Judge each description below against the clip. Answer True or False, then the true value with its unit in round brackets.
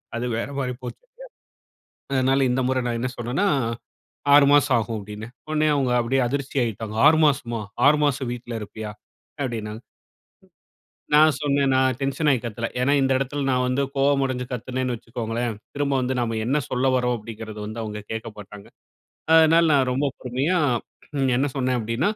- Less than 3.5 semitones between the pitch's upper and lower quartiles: True (3.1 semitones)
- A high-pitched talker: False (125 Hz)